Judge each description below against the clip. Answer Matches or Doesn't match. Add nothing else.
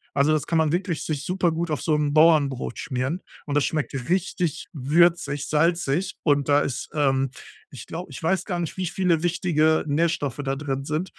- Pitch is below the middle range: Doesn't match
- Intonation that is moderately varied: Matches